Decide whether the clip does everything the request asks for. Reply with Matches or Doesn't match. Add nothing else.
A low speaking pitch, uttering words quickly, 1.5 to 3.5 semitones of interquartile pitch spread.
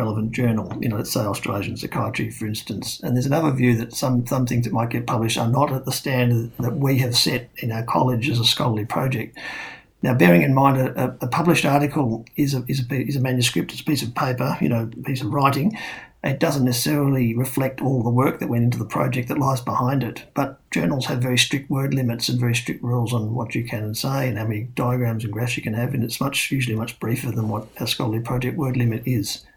Matches